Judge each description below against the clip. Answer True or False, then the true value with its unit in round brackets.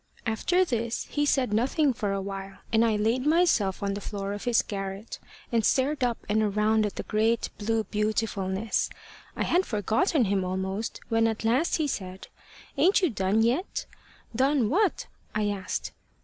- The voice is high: True (220 Hz)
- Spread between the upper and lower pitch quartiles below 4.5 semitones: True (4.0 semitones)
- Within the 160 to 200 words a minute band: True (170 wpm)